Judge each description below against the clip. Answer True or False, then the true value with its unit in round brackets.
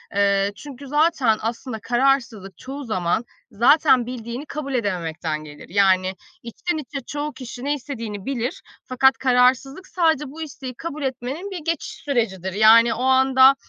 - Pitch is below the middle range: False (255 Hz)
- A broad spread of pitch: False (4.5 semitones)